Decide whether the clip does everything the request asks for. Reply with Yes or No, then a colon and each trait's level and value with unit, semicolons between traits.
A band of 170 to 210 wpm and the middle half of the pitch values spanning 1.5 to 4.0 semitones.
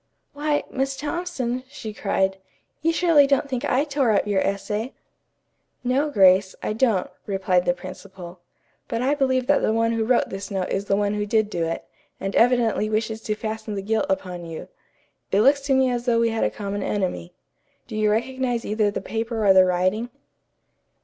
No: average, 190 wpm; average, 4.6 semitones